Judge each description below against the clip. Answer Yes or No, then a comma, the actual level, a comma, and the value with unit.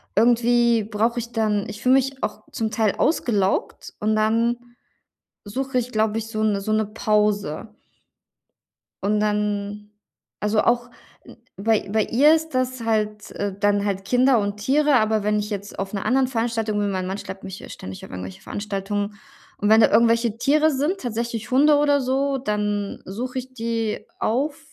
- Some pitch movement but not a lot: Yes, average, 3.1 semitones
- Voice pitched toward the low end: No, high, 220 Hz